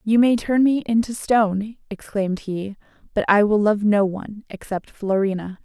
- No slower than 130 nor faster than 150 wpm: No, average, 170 wpm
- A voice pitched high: Yes, high, 210 Hz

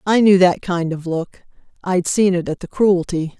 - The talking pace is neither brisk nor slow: Yes, average, 195 wpm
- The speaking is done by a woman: Yes, female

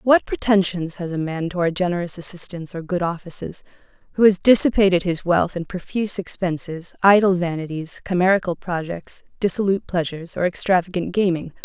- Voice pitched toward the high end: No, medium, 180 Hz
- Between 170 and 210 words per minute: No, average, 150 wpm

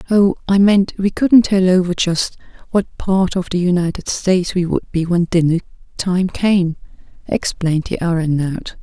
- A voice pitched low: No, medium, 180 Hz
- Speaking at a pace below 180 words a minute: Yes, average, 165 wpm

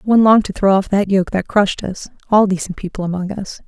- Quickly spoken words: Yes, fast, 245 wpm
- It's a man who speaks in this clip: No, female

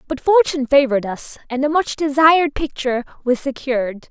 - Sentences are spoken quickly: No, average, 160 wpm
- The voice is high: Yes, very high, 275 Hz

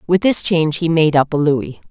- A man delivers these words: No, female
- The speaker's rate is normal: No, fast, 250 wpm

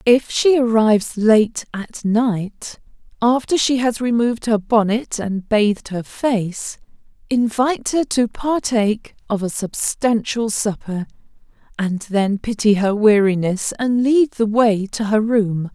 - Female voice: Yes, female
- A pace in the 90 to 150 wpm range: Yes, slow, 135 wpm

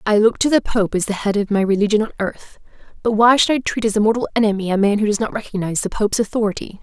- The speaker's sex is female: Yes, female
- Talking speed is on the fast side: Yes, fast, 275 wpm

